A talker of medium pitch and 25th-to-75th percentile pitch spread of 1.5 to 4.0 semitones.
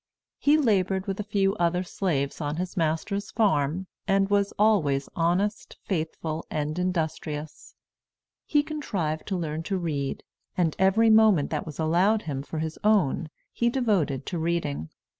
No: medium, 180 Hz; average, 4.5 semitones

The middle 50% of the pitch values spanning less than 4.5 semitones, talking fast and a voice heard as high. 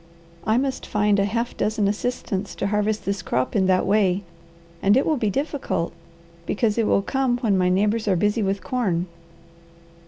No: average, 3.0 semitones; average, 180 wpm; high, 210 Hz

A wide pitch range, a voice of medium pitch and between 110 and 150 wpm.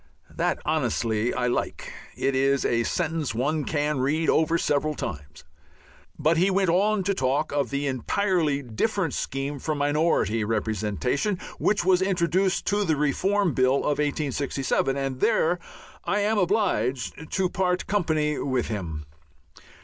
Yes: wide, 5.7 semitones; medium, 150 Hz; average, 140 wpm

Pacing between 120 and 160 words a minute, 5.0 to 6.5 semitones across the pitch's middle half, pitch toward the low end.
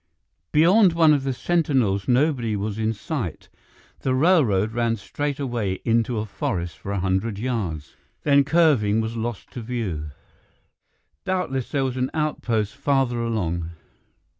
Yes: average, 140 wpm; average, 5.3 semitones; low, 120 Hz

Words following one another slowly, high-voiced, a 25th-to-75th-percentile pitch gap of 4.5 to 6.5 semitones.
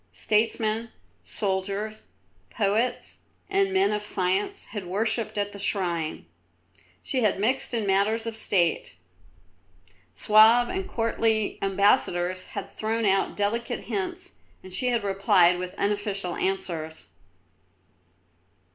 No: slow, 110 wpm; high, 205 Hz; average, 2.9 semitones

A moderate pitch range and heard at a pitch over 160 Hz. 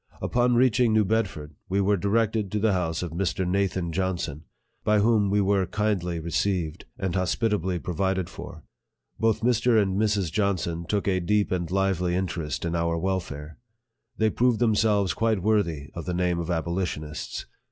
No: average, 3.6 semitones; very low, 95 Hz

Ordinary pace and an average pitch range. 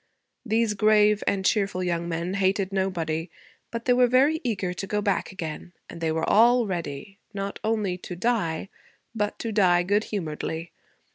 Yes: average, 165 wpm; average, 3.6 semitones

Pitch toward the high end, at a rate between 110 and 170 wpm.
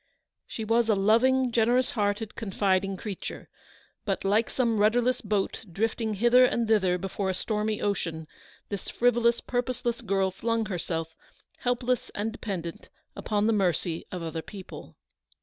Yes: high, 215 Hz; average, 140 wpm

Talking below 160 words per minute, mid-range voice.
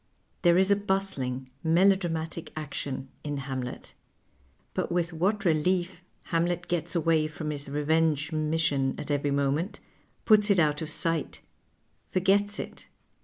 Yes: average, 140 wpm; medium, 160 Hz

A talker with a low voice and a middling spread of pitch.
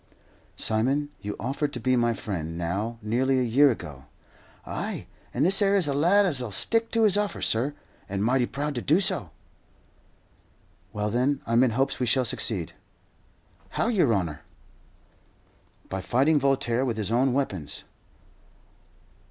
Yes: low, 125 Hz; average, 4.8 semitones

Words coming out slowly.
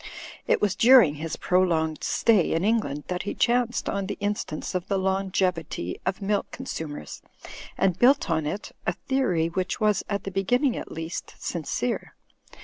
No: average, 165 wpm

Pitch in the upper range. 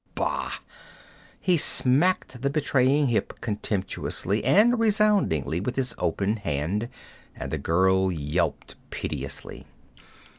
No: low, 115 Hz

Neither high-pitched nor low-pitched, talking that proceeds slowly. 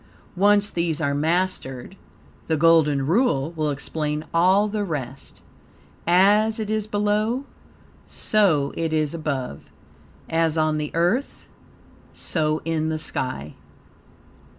Yes: medium, 165 Hz; slow, 115 wpm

